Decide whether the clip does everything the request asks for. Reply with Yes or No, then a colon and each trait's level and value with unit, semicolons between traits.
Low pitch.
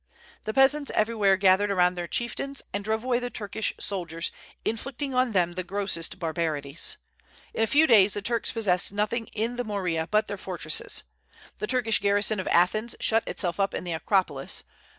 No: high, 205 Hz